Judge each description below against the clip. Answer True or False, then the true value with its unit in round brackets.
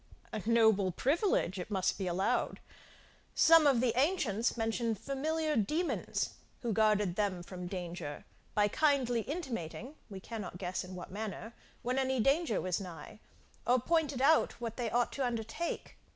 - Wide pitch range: True (5.8 semitones)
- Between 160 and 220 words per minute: False (150 wpm)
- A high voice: True (225 Hz)